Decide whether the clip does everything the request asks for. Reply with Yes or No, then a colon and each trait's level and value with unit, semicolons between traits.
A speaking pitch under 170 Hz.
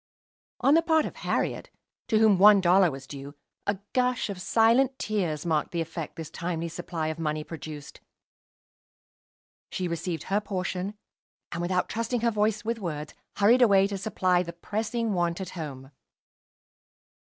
No: medium, 185 Hz